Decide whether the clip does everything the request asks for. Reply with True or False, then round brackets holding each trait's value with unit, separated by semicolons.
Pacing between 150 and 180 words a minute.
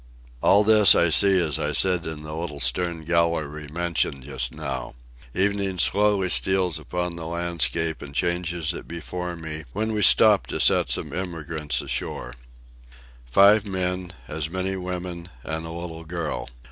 True (155 wpm)